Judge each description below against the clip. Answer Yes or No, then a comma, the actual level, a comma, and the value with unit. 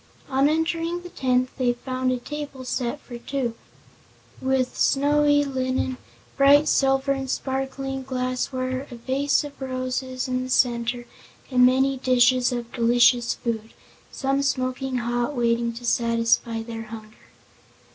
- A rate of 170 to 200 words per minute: No, slow, 135 wpm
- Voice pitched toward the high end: Yes, very high, 255 Hz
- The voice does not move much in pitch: Yes, narrow, 2.0 semitones